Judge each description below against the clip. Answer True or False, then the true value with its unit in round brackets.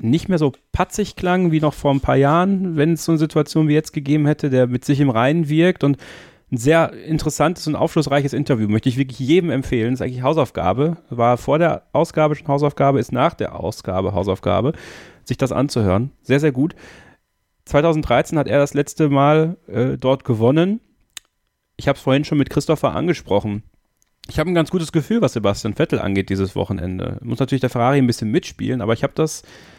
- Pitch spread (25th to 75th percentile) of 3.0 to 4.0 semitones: False (4.5 semitones)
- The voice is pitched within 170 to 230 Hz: False (140 Hz)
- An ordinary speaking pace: False (200 wpm)